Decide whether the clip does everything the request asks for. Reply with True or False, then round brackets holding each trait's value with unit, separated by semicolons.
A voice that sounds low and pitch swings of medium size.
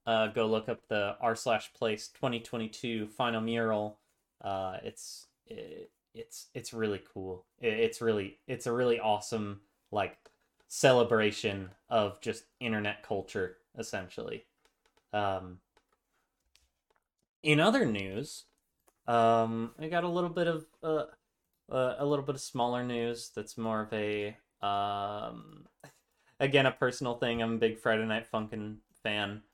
True (115 Hz; 3.5 semitones)